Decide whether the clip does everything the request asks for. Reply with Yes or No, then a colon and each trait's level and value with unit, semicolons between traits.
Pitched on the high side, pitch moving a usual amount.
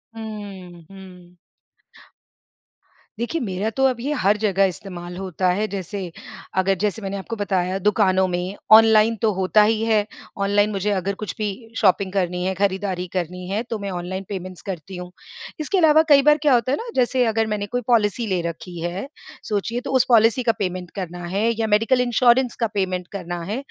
Yes: high, 200 Hz; average, 3.4 semitones